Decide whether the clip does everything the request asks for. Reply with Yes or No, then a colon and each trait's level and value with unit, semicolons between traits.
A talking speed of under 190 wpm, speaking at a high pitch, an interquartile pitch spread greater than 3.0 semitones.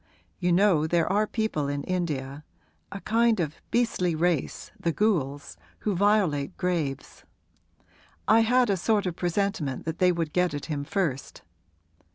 No: average, 150 wpm; medium, 175 Hz; average, 5.2 semitones